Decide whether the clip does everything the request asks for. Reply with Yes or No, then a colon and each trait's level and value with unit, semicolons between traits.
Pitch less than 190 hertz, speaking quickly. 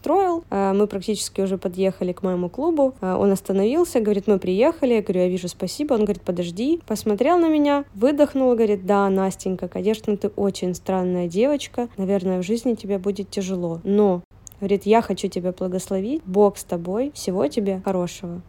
No: high, 200 Hz; fast, 165 wpm